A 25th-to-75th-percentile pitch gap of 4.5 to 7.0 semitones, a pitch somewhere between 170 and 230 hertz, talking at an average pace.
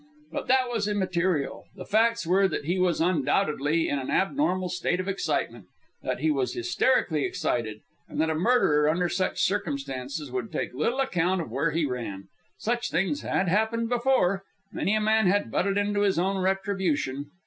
Yes: wide, 5.5 semitones; medium, 185 Hz; average, 175 wpm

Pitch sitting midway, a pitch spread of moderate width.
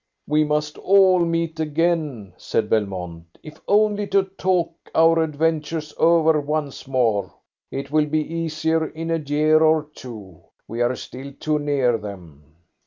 Yes: medium, 155 Hz; average, 4.5 semitones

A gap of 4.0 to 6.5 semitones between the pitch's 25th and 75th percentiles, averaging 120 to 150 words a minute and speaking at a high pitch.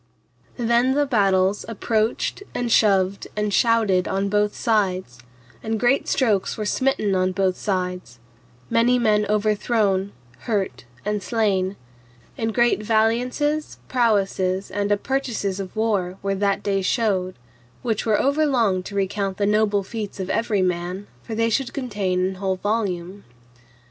No: average, 3.1 semitones; average, 140 wpm; high, 205 Hz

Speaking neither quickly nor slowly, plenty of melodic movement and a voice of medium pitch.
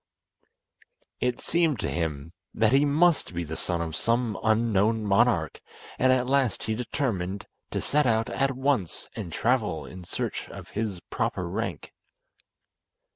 No: average, 145 wpm; wide, 6.0 semitones; low, 110 Hz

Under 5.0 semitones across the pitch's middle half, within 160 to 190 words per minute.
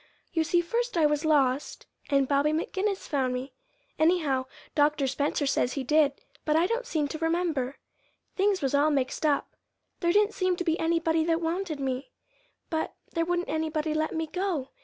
Yes: average, 3.4 semitones; average, 180 wpm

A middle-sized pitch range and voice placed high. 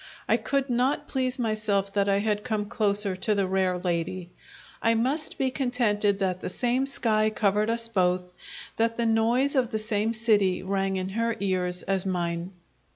Yes: average, 3.4 semitones; high, 210 Hz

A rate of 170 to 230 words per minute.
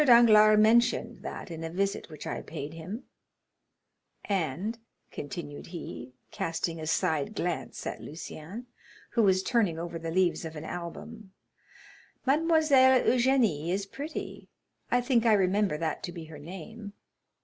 No: average, 140 wpm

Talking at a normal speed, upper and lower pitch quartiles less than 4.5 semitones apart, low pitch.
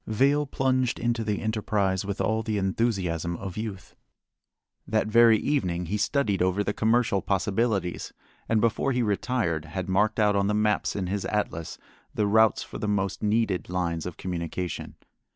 Yes: average, 165 wpm; average, 3.1 semitones; low, 105 Hz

